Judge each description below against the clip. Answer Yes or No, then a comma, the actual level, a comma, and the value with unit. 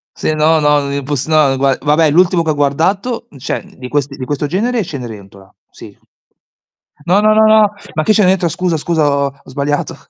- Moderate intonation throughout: Yes, average, 4.5 semitones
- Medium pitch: Yes, medium, 150 Hz